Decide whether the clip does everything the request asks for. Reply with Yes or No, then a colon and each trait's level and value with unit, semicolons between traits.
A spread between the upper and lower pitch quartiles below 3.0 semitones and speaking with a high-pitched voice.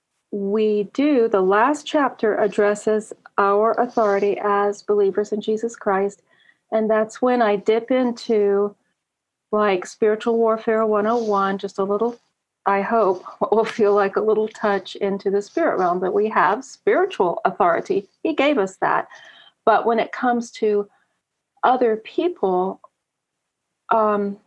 Yes: narrow, 2.4 semitones; high, 215 Hz